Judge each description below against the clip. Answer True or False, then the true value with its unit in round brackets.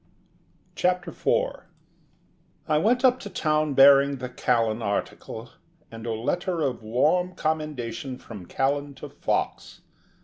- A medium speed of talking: False (125 wpm)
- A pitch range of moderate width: False (6.5 semitones)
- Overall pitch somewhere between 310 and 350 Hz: False (140 Hz)